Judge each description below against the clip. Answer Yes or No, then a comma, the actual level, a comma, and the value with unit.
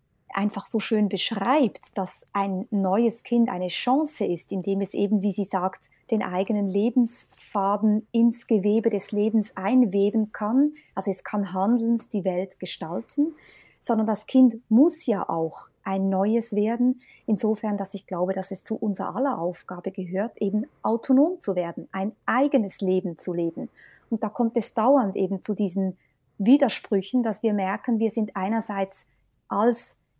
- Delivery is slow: No, average, 155 wpm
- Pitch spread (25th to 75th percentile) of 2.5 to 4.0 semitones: Yes, average, 3.2 semitones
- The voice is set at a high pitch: Yes, high, 210 Hz